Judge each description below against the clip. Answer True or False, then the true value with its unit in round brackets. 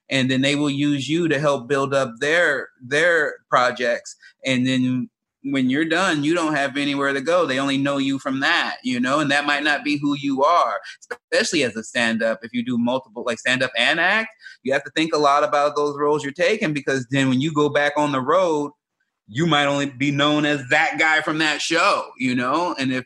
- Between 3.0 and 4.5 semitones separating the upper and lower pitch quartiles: False (2.5 semitones)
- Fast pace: True (230 wpm)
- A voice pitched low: False (145 Hz)